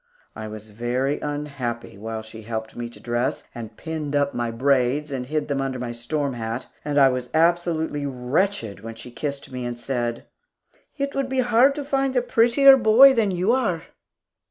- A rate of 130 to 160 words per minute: No, average, 190 wpm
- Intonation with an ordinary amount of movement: No, wide, 6.9 semitones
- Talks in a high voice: No, medium, 140 Hz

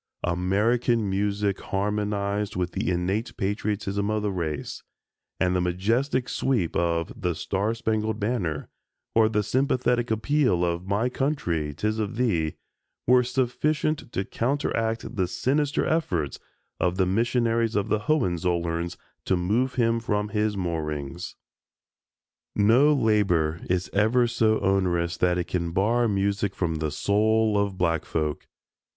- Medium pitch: No, low, 105 Hz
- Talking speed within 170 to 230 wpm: No, slow, 135 wpm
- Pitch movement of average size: Yes, average, 4.5 semitones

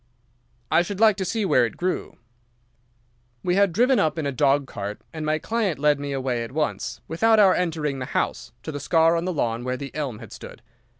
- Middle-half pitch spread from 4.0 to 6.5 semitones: Yes, average, 5.2 semitones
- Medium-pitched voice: Yes, medium, 155 Hz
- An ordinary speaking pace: No, fast, 220 wpm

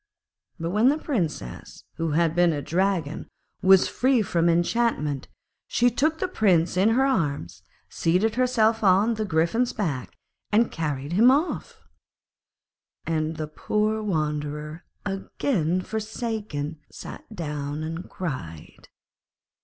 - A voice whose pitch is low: No, medium, 180 Hz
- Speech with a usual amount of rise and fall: No, wide, 6.1 semitones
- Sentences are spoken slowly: Yes, slow, 120 wpm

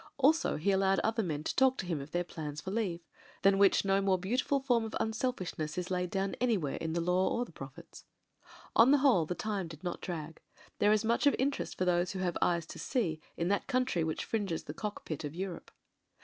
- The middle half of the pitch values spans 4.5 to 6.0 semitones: Yes, average, 4.8 semitones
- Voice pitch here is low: No, high, 190 Hz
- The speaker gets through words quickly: Yes, fast, 235 wpm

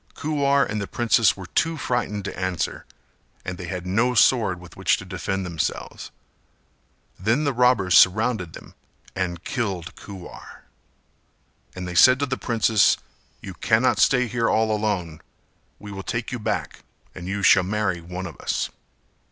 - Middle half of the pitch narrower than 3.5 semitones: No, average, 4.6 semitones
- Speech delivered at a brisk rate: No, average, 160 wpm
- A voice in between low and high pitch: No, low, 100 Hz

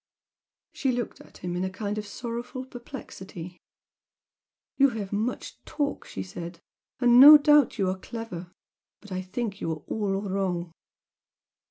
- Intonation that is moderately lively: Yes, average, 4.8 semitones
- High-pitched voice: Yes, high, 205 Hz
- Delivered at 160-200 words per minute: No, average, 150 wpm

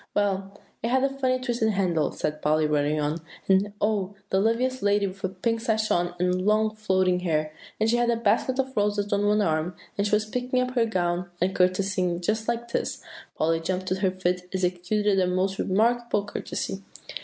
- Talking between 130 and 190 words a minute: No, average, 200 wpm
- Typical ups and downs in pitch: Yes, average, 3.4 semitones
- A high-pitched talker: Yes, high, 200 Hz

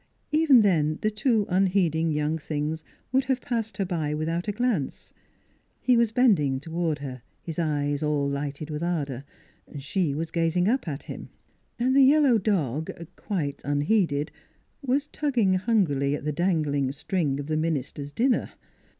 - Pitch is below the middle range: No, medium, 165 Hz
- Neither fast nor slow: Yes, average, 155 wpm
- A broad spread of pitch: Yes, wide, 6.6 semitones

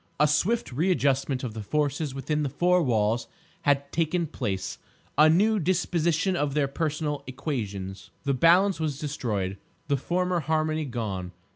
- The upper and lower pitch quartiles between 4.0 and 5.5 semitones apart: Yes, average, 4.6 semitones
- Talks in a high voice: No, medium, 150 Hz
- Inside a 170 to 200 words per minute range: No, average, 140 wpm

